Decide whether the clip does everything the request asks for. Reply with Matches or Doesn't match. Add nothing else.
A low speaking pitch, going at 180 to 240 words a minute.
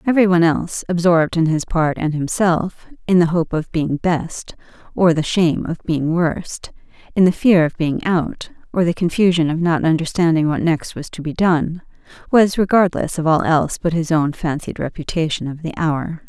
Doesn't match